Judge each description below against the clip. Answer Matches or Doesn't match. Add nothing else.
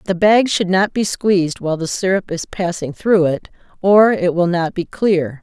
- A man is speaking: Doesn't match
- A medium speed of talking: Doesn't match